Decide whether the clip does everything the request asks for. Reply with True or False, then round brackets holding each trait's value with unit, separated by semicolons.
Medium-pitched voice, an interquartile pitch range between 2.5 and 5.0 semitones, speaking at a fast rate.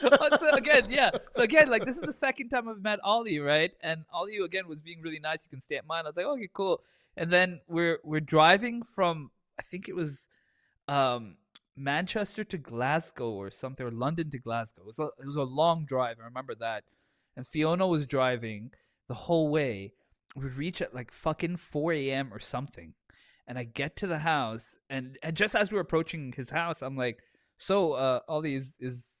False (155 Hz; 5.6 semitones; 210 wpm)